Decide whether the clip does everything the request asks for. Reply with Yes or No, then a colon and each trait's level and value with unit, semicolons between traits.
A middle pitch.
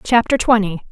No: high, 215 Hz